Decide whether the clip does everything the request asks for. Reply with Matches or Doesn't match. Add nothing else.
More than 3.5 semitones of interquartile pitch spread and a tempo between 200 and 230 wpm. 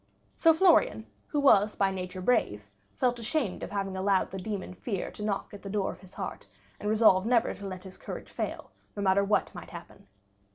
Doesn't match